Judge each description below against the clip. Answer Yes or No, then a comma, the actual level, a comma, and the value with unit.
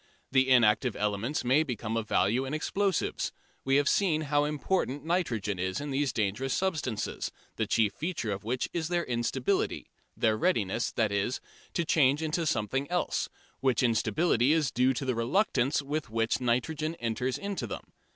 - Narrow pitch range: No, average, 5.3 semitones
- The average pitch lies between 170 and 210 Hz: No, low, 130 Hz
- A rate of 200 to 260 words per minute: No, average, 165 wpm